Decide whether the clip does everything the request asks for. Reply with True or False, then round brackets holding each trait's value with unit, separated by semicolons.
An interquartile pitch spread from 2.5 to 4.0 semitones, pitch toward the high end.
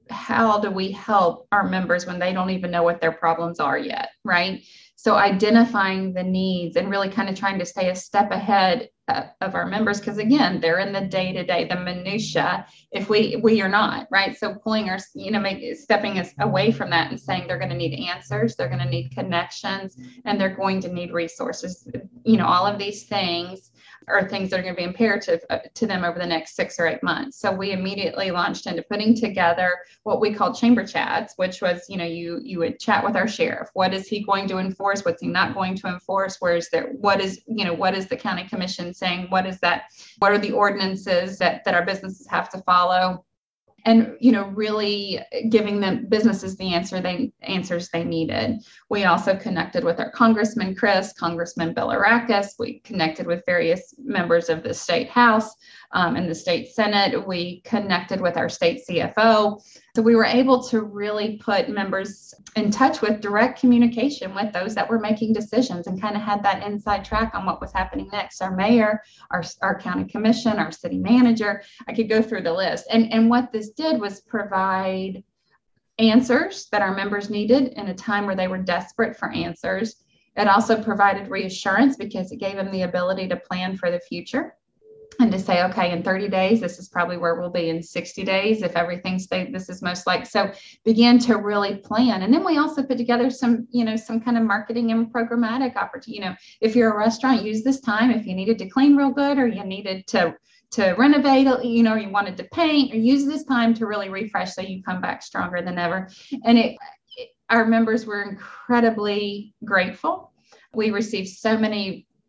True (3.5 semitones; 200 Hz)